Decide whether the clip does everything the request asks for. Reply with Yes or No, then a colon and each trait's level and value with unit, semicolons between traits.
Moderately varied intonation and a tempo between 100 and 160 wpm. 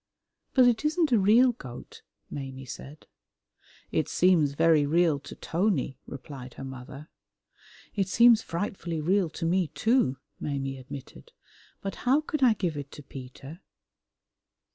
No: wide, 7.5 semitones; average, 140 wpm